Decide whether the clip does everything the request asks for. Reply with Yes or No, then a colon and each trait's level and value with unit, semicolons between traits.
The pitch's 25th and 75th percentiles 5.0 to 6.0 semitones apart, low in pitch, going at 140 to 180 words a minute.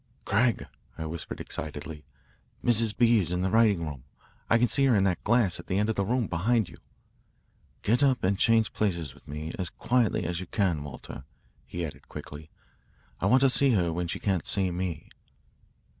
No: wide, 5.4 semitones; very low, 95 Hz; average, 195 wpm